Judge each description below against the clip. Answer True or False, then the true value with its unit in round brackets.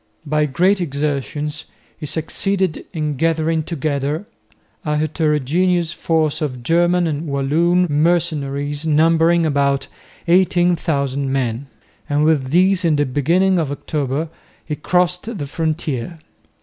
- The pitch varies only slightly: False (3.2 semitones)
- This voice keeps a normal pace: False (115 wpm)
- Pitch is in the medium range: True (155 Hz)